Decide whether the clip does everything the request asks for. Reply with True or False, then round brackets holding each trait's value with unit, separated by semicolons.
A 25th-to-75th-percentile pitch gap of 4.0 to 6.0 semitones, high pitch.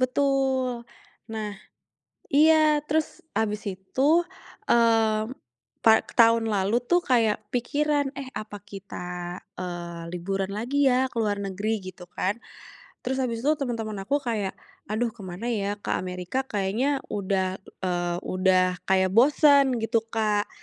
True (5.1 semitones; 220 Hz)